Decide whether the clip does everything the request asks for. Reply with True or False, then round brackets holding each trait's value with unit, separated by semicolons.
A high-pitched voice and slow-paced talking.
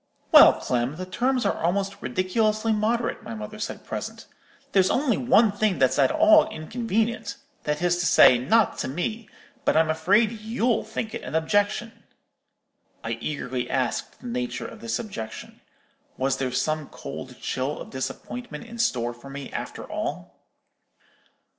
False (195 Hz; 155 wpm)